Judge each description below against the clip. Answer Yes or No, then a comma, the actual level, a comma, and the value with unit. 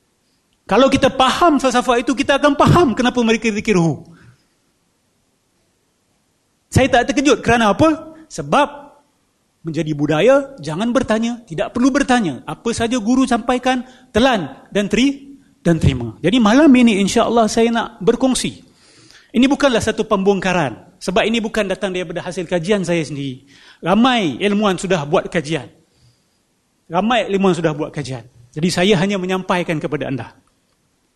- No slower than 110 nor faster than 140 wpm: Yes, average, 135 wpm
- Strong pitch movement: Yes, wide, 7.1 semitones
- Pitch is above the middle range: Yes, high, 215 Hz